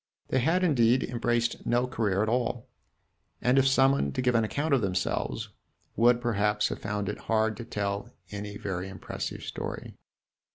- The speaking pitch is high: No, low, 115 Hz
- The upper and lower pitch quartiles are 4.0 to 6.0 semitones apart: No, average, 3.4 semitones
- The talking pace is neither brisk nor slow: Yes, average, 165 wpm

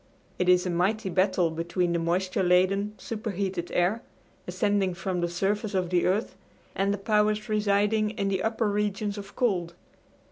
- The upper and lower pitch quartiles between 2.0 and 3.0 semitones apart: Yes, narrow, 2.6 semitones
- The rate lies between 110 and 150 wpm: No, average, 165 wpm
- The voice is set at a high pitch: Yes, high, 195 Hz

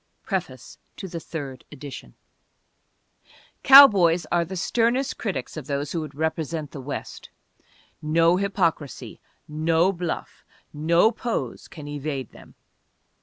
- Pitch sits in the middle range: Yes, medium, 165 Hz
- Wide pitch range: No, average, 3.8 semitones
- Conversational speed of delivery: No, slow, 120 wpm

